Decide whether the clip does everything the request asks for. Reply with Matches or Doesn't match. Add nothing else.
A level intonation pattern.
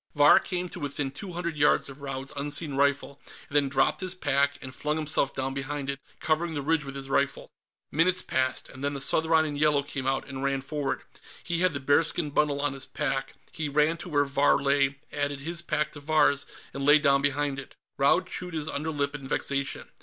Matches